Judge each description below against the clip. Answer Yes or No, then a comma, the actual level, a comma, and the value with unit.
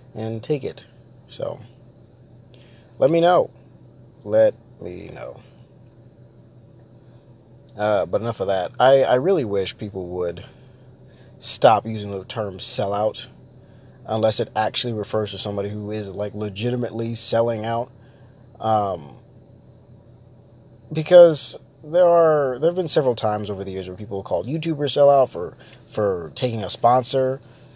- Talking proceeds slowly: Yes, slow, 130 wpm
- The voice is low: Yes, low, 120 Hz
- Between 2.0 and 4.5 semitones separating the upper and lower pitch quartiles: Yes, average, 3.4 semitones